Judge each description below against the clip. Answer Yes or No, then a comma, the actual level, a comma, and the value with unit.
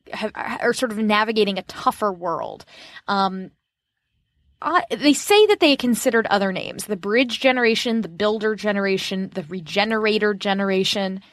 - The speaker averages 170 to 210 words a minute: No, average, 140 wpm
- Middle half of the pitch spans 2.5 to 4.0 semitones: Yes, average, 3.3 semitones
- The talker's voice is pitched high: Yes, high, 210 Hz